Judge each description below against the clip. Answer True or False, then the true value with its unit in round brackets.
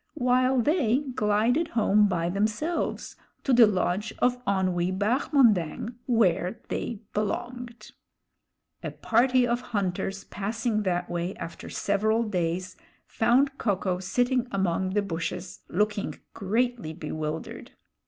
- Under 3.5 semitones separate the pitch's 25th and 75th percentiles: False (4.7 semitones)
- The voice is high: True (210 Hz)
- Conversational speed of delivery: False (115 wpm)